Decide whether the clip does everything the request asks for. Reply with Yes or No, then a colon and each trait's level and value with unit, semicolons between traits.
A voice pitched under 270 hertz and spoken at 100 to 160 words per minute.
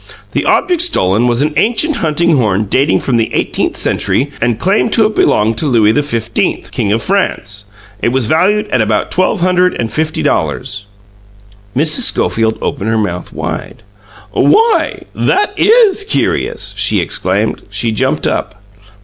Yes: low, 135 Hz; average, 155 wpm